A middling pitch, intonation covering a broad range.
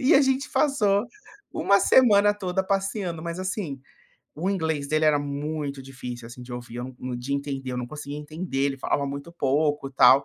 Yes: medium, 150 Hz; wide, 5.9 semitones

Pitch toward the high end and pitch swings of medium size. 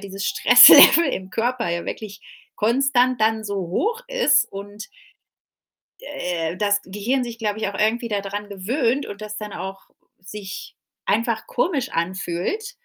Yes: high, 210 Hz; average, 3.7 semitones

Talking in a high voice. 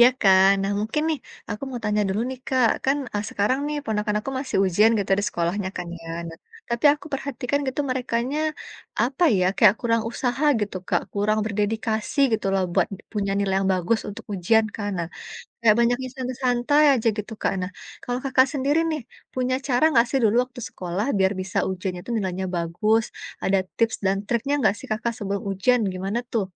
Yes: high, 220 Hz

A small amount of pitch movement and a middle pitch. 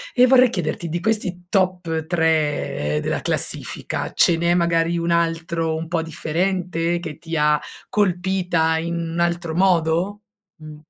Yes: narrow, 1.8 semitones; medium, 170 Hz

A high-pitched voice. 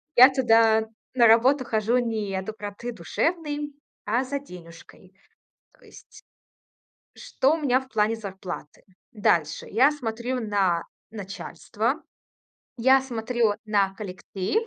Yes: high, 225 Hz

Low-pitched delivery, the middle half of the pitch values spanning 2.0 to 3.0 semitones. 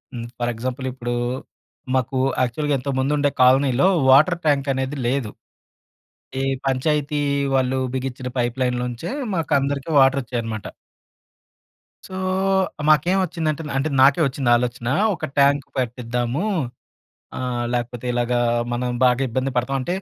Yes: low, 130 Hz; narrow, 2.5 semitones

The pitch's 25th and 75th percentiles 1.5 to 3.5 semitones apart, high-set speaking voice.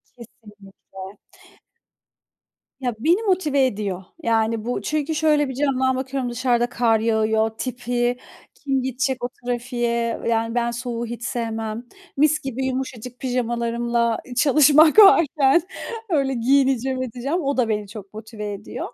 Yes: average, 2.8 semitones; high, 245 Hz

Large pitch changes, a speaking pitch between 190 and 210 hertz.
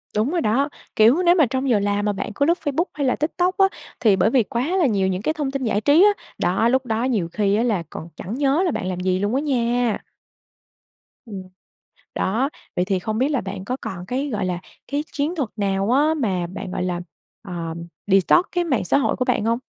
No: wide, 6.4 semitones; high, 230 Hz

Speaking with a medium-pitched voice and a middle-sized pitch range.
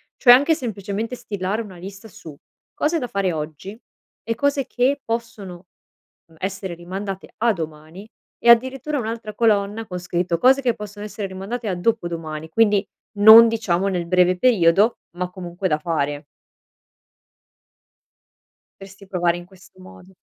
No: high, 195 Hz; average, 4.3 semitones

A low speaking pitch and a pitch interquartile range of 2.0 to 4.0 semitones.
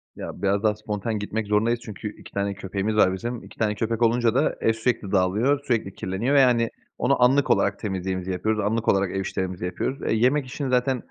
Yes: low, 110 Hz; average, 3.7 semitones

